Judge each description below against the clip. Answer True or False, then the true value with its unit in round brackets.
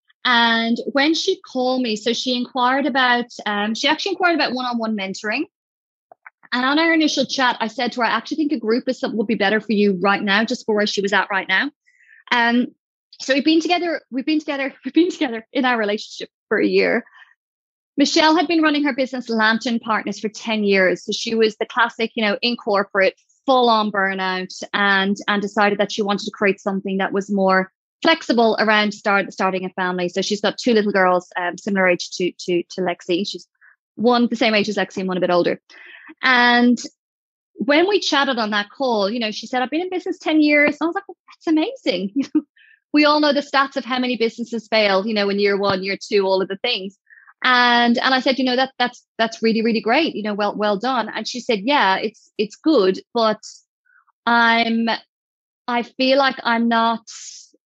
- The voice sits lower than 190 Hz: False (230 Hz)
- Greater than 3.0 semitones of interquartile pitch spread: True (4.9 semitones)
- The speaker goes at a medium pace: False (210 wpm)